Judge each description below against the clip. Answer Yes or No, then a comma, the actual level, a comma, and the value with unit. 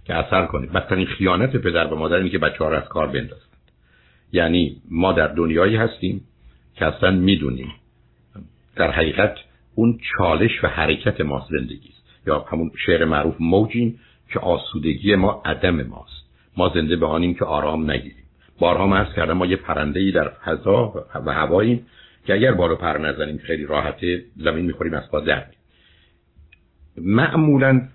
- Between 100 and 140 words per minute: No, fast, 155 wpm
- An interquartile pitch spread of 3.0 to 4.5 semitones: No, average, 4.9 semitones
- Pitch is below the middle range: Yes, very low, 85 Hz